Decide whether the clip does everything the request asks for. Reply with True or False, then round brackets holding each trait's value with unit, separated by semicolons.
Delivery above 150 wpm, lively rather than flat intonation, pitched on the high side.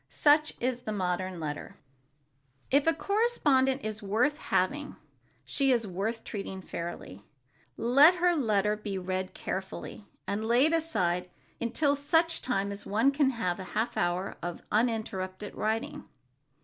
False (135 wpm; 6.8 semitones; 220 Hz)